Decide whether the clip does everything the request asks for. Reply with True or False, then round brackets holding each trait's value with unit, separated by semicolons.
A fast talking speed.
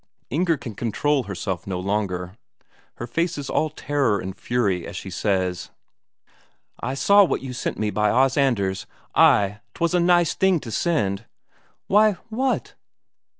False (150 wpm)